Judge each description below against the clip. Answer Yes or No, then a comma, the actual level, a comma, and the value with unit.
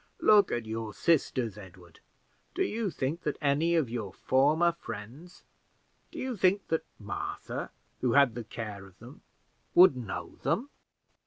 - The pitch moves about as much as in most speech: No, wide, 7.3 semitones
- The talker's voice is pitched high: No, low, 130 Hz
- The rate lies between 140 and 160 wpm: Yes, average, 150 wpm